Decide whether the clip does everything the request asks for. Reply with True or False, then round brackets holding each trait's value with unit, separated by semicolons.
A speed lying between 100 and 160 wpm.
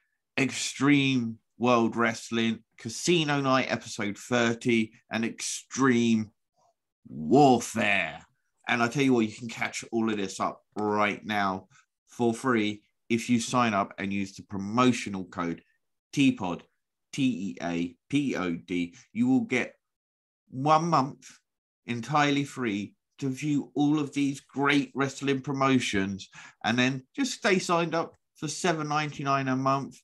True (135 wpm)